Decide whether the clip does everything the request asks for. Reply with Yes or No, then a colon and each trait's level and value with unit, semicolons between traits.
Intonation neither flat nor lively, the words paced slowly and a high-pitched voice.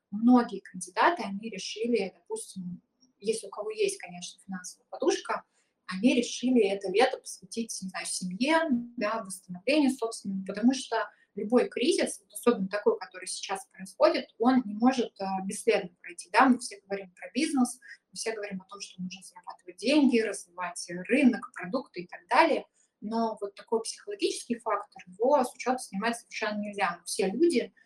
No: average, 4.4 semitones; average, 155 wpm; high, 220 Hz